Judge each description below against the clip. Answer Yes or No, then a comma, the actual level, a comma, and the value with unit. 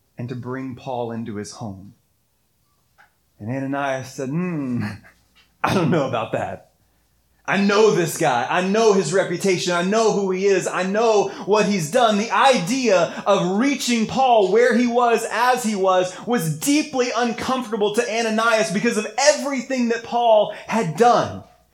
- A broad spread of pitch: Yes, wide, 7.7 semitones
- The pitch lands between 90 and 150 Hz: No, high, 205 Hz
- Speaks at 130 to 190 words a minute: Yes, average, 155 wpm